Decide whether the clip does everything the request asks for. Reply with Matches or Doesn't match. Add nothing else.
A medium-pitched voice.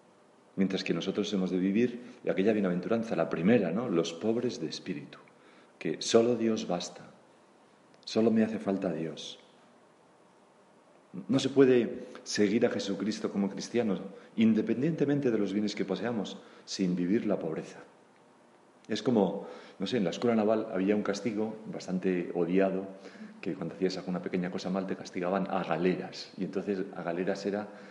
Doesn't match